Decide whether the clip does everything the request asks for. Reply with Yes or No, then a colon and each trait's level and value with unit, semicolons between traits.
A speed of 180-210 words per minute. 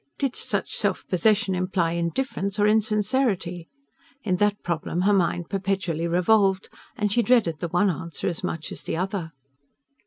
No: average, 155 wpm